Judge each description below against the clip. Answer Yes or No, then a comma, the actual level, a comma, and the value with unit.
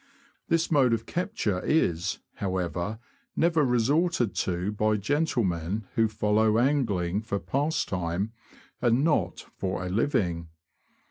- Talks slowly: Yes, slow, 115 wpm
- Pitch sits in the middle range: No, low, 110 Hz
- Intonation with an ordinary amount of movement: No, wide, 7.1 semitones